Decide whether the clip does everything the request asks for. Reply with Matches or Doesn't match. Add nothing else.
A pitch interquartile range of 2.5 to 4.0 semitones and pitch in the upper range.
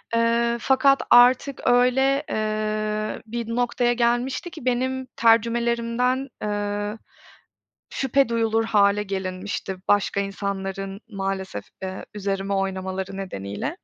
Matches